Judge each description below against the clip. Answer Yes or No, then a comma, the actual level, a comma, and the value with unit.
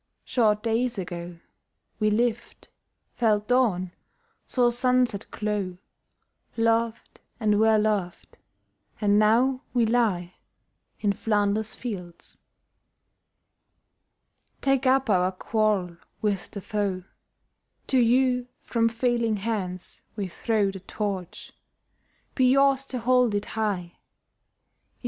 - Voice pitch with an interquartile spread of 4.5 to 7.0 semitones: No, average, 3.3 semitones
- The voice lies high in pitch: Yes, high, 215 Hz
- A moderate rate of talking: No, slow, 105 wpm